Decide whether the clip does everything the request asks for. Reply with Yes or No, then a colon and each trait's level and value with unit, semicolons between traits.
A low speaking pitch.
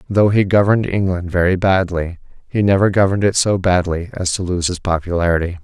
Yes: very low, 95 Hz